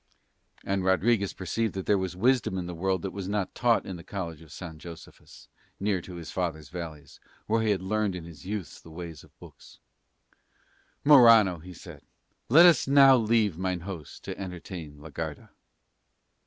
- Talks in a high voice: No, very low, 95 Hz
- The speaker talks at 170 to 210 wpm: Yes, average, 180 wpm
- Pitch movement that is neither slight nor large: Yes, average, 3.9 semitones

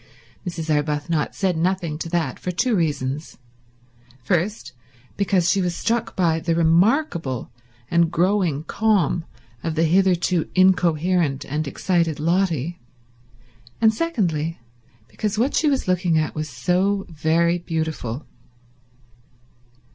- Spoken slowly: Yes, slow, 115 wpm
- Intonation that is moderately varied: Yes, average, 3.4 semitones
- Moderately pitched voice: Yes, medium, 170 Hz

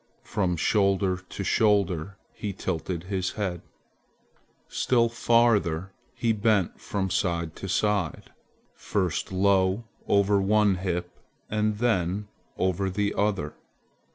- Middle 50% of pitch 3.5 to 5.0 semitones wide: No, narrow, 2.4 semitones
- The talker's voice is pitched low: Yes, very low, 95 Hz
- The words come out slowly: Yes, slow, 110 wpm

